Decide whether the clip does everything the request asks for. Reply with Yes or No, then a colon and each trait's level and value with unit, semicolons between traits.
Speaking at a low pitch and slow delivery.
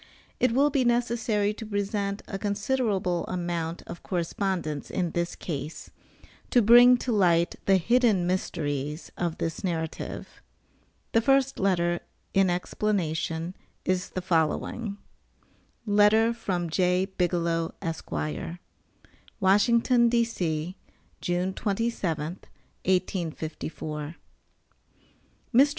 No: medium, 185 Hz; slow, 100 wpm